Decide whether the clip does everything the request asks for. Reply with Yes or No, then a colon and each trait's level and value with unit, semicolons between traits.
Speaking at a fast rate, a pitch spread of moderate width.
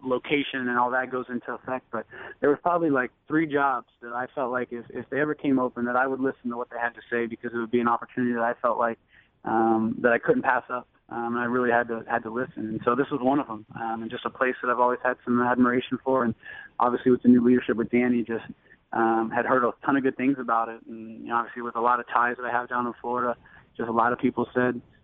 No: fast, 285 wpm; narrow, 1.4 semitones